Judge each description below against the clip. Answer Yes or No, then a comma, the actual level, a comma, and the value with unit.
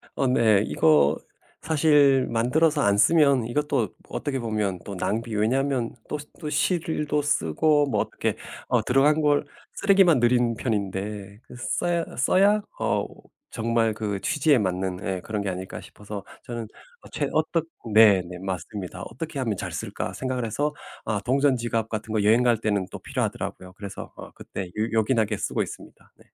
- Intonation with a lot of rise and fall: Yes, wide, 5.9 semitones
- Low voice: Yes, low, 115 Hz